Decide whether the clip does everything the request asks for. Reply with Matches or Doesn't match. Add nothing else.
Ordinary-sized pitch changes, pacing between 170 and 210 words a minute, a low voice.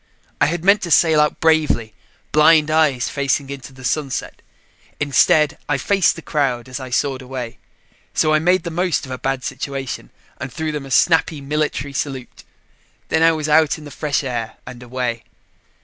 Doesn't match